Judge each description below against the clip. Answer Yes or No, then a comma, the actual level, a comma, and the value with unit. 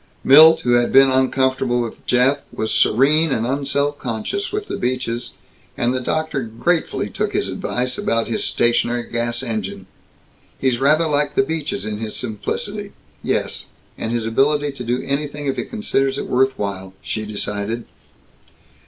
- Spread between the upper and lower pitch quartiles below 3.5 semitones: No, average, 3.8 semitones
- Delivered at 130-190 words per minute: Yes, average, 160 wpm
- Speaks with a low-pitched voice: Yes, low, 130 Hz